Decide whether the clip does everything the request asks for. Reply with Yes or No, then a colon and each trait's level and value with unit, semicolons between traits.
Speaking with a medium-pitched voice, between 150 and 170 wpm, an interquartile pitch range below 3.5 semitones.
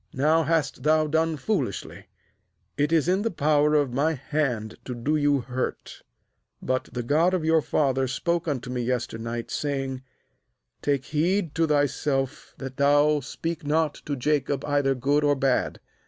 Yes: medium, 145 Hz; average, 160 wpm; average, 2.9 semitones